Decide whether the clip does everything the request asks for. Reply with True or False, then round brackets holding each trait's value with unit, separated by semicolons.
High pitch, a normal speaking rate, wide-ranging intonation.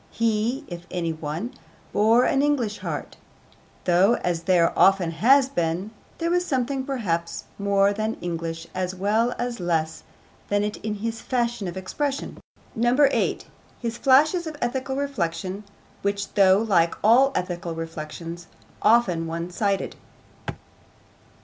False (205 Hz; 130 wpm; 5.9 semitones)